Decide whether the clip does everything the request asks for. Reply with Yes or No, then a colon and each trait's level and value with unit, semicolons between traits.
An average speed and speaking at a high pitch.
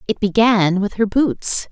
Yes: average, 175 wpm; high, 210 Hz